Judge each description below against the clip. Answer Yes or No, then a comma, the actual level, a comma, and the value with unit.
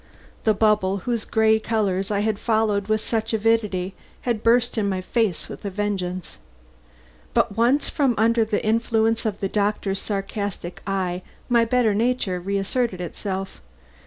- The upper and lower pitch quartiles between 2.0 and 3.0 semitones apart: Yes, narrow, 2.6 semitones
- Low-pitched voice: No, high, 210 Hz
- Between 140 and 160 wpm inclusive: Yes, average, 150 wpm